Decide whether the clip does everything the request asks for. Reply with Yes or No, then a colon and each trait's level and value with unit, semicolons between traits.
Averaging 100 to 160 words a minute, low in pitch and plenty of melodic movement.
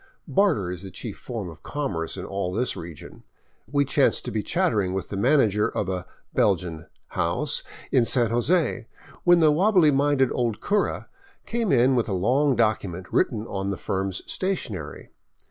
No: average, 175 wpm; low, 115 Hz; wide, 7.3 semitones